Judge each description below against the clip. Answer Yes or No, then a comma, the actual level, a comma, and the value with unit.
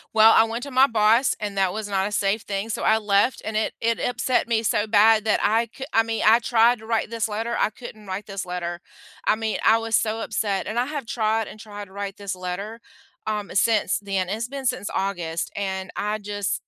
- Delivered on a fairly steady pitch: Yes, narrow, 2.2 semitones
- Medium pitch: No, high, 215 Hz